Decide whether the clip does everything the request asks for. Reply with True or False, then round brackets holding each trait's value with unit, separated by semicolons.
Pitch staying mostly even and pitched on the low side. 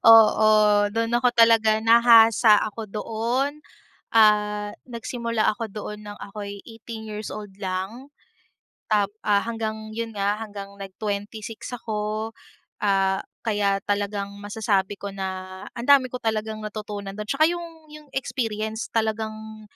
False (1.8 semitones; 215 Hz)